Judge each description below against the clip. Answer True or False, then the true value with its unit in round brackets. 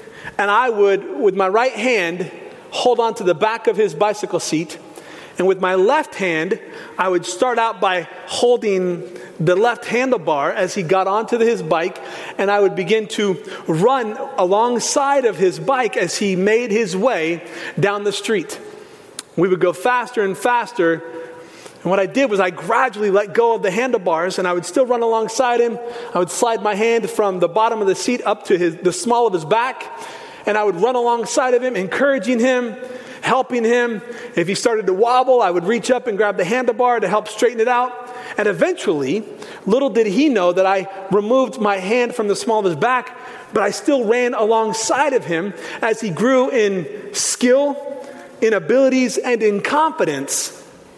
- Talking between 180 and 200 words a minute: True (190 wpm)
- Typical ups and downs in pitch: True (4.5 semitones)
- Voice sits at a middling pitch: False (230 Hz)